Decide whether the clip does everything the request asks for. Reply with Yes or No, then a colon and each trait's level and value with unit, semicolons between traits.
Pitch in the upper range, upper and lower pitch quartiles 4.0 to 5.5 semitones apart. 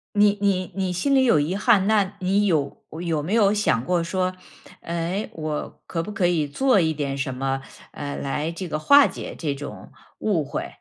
No: medium, 175 Hz; average, 5.1 semitones